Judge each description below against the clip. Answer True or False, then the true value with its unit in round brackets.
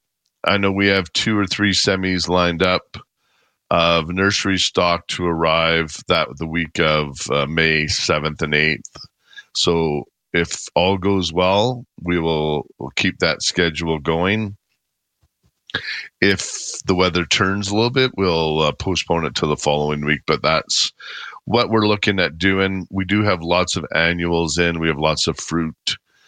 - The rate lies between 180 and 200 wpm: False (160 wpm)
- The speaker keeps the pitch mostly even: False (3.2 semitones)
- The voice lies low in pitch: True (90 Hz)